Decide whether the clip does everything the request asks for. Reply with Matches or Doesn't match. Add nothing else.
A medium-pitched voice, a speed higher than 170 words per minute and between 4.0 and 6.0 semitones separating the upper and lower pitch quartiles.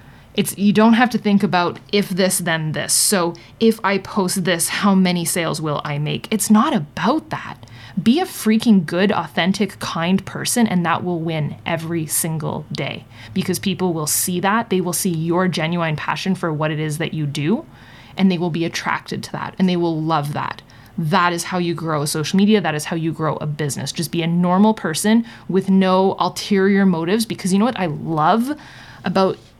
Doesn't match